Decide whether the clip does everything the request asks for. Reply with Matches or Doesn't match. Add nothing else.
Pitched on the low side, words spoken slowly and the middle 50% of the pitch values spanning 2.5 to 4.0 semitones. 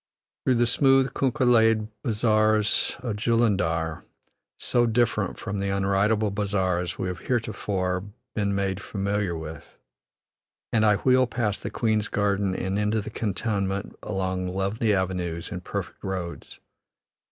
Matches